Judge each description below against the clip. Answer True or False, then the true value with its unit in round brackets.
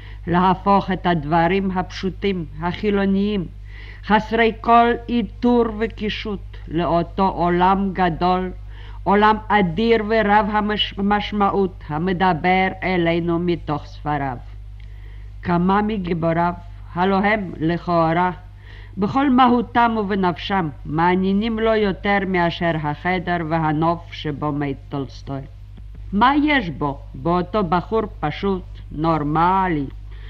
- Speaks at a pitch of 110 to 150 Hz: False (180 Hz)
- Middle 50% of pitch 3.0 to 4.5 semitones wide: False (5.3 semitones)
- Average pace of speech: False (90 wpm)